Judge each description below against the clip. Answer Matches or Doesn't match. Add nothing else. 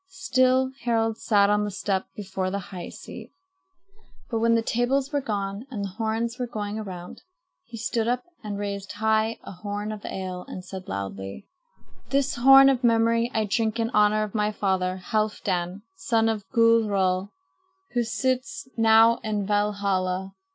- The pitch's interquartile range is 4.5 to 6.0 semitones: Doesn't match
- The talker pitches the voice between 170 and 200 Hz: Doesn't match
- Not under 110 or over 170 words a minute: Matches